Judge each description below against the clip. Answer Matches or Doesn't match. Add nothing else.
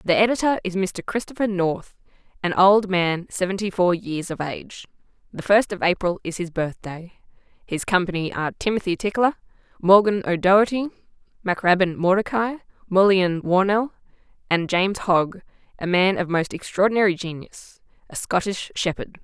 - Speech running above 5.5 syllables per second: Doesn't match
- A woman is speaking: Matches